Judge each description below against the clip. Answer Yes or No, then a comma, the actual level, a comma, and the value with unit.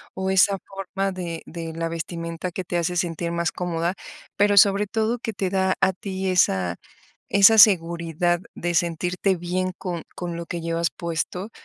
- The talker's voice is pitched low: No, medium, 180 Hz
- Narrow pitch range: Yes, narrow, 2.3 semitones